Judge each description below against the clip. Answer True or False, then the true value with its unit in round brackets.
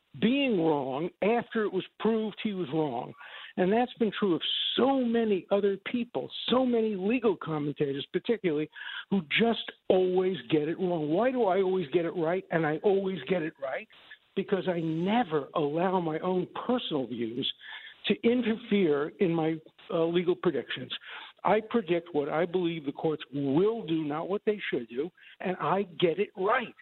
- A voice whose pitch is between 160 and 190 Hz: True (185 Hz)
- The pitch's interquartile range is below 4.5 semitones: False (5.0 semitones)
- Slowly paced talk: False (170 wpm)